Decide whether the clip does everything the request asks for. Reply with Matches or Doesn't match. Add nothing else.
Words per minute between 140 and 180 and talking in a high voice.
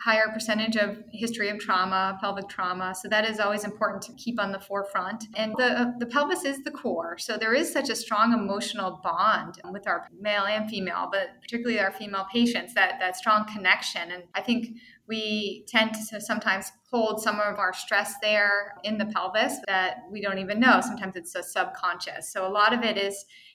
Doesn't match